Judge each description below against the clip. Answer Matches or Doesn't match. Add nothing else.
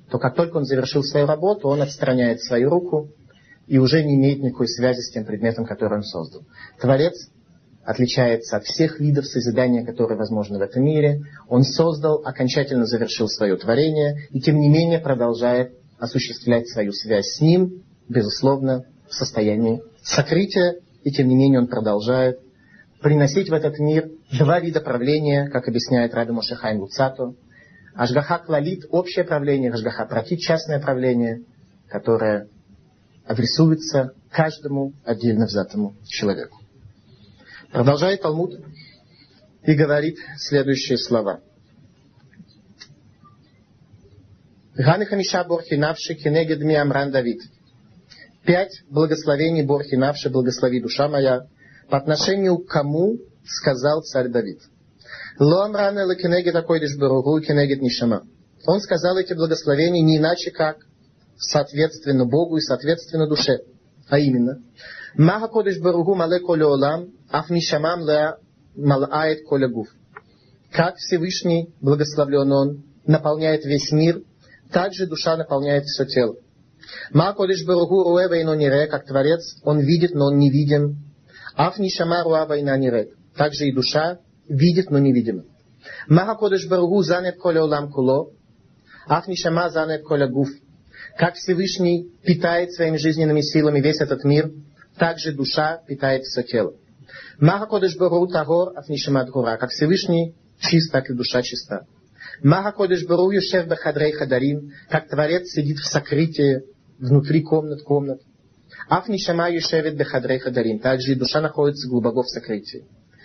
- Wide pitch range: Doesn't match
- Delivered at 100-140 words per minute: Matches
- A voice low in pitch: Doesn't match